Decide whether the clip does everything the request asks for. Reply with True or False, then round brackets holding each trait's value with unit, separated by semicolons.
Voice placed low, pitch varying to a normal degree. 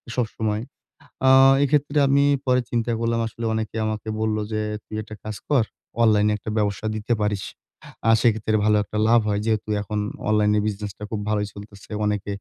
False (110 Hz; 1.7 semitones)